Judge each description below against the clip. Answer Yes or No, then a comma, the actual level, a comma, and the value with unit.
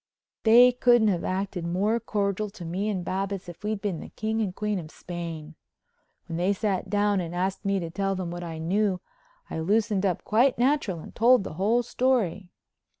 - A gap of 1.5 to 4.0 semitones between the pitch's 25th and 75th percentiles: Yes, average, 3.5 semitones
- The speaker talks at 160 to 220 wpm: Yes, average, 195 wpm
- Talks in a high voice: Yes, high, 195 Hz